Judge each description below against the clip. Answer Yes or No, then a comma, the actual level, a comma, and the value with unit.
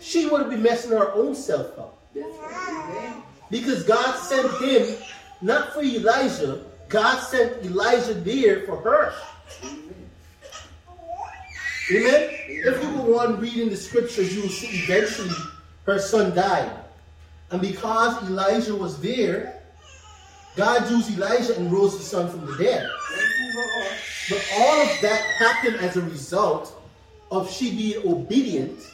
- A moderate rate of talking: No, slow, 130 wpm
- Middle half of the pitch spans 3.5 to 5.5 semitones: Yes, average, 5.1 semitones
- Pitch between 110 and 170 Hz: No, high, 225 Hz